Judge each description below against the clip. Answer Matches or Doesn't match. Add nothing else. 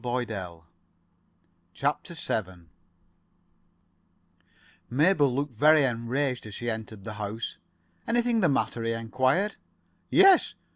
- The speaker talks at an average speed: Doesn't match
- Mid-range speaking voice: Doesn't match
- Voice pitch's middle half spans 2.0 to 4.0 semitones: Doesn't match